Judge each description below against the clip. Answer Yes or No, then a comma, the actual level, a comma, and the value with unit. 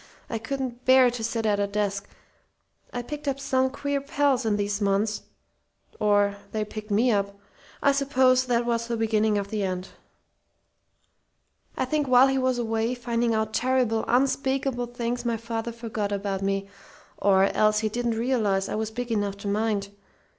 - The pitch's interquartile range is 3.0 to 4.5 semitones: Yes, average, 3.5 semitones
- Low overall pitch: No, high, 230 Hz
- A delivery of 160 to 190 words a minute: Yes, average, 170 wpm